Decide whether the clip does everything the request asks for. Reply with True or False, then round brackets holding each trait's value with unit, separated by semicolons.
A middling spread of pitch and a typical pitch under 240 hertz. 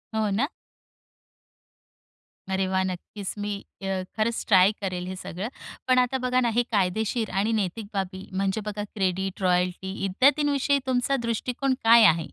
True (3.8 semitones; 205 Hz)